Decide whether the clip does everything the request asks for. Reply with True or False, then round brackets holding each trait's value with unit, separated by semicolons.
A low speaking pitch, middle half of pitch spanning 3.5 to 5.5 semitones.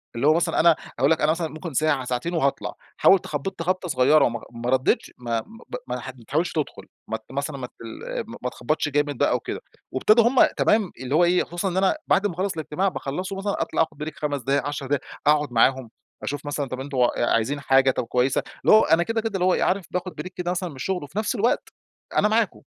False (155 Hz; 5.2 semitones)